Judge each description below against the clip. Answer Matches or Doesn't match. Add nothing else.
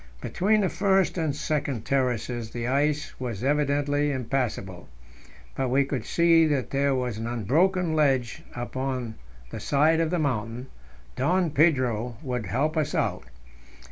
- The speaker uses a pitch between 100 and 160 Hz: Matches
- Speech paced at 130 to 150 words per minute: Matches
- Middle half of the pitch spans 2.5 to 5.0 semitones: Matches